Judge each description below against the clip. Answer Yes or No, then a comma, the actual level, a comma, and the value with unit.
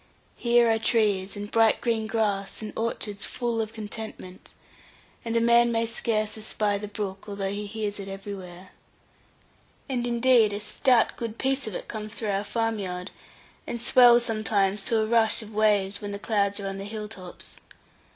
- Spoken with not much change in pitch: Yes, narrow, 2.2 semitones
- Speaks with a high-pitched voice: Yes, high, 215 Hz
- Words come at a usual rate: Yes, average, 180 wpm